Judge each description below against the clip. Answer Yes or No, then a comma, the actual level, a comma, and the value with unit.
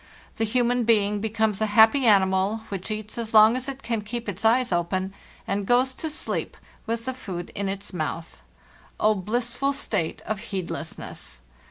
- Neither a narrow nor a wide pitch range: Yes, average, 3.5 semitones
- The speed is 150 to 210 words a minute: Yes, average, 170 wpm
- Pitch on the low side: No, high, 215 Hz